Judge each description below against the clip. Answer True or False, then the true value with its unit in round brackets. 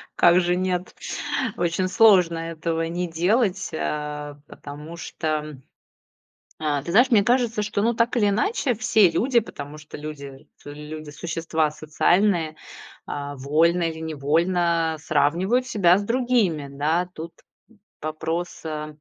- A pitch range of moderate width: True (4.4 semitones)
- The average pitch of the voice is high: False (165 Hz)